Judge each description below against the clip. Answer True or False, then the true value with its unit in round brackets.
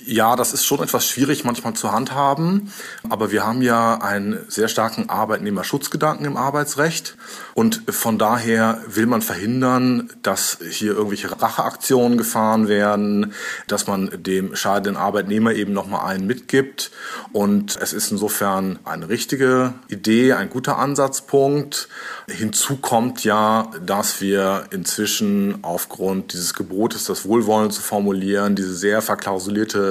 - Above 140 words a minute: False (130 wpm)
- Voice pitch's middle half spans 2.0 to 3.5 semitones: False (3.9 semitones)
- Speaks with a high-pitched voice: False (110 Hz)